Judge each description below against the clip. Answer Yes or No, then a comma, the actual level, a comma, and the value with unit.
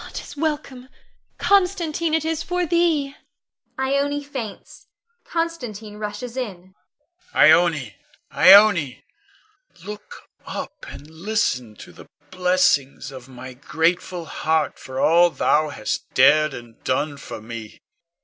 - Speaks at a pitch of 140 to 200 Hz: Yes, medium, 185 Hz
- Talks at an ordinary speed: No, slow, 120 wpm